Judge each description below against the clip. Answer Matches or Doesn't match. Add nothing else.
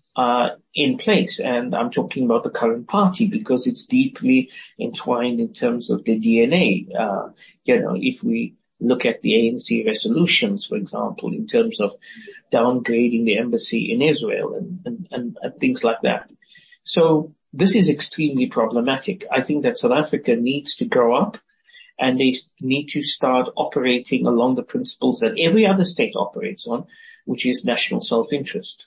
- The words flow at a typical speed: Matches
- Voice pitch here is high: Matches